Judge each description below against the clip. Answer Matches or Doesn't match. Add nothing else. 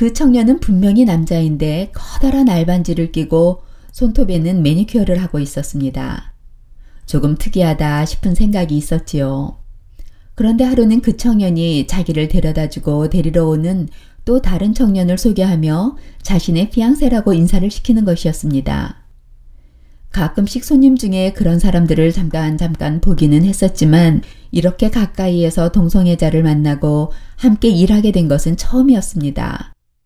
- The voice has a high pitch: Doesn't match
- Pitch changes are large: Doesn't match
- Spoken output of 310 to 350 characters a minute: Matches